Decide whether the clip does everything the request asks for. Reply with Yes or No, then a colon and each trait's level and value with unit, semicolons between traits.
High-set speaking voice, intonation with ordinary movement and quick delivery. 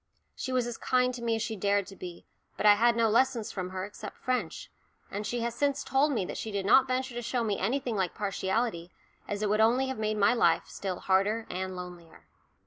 Yes: high, 220 Hz; average, 3.9 semitones; fast, 230 wpm